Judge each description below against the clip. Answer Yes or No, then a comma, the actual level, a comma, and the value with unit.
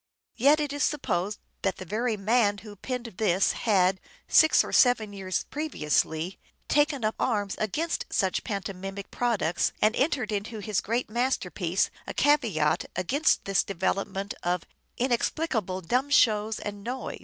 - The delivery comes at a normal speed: Yes, average, 155 wpm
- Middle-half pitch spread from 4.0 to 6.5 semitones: Yes, average, 4.6 semitones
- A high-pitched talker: Yes, high, 210 Hz